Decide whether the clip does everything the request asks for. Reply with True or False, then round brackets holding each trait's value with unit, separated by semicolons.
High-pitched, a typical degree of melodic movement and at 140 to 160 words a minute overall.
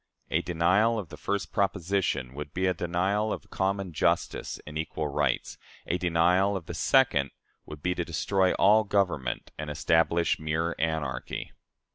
False (85 Hz; 3.8 semitones; 155 wpm)